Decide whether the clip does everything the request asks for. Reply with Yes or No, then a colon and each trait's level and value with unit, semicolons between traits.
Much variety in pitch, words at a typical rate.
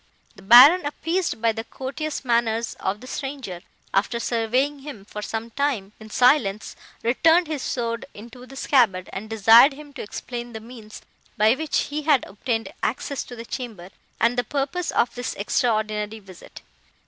No: average, 4.0 semitones; average, 165 wpm